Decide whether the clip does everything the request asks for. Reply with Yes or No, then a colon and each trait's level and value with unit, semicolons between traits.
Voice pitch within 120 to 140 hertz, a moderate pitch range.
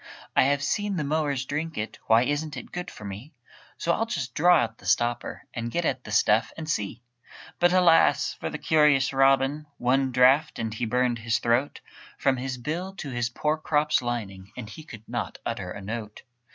Yes: low, 135 Hz; average, 4.6 semitones